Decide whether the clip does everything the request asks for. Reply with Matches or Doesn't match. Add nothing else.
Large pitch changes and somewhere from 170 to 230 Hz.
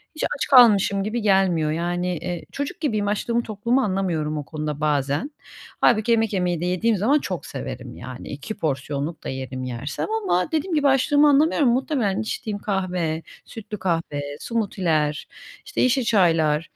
Matches